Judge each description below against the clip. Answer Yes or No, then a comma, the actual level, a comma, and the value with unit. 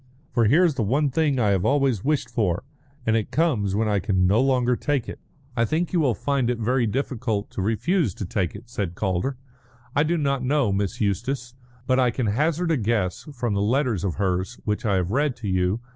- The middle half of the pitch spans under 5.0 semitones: No, average, 5.3 semitones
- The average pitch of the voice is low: Yes, low, 120 Hz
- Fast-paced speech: Yes, fast, 220 wpm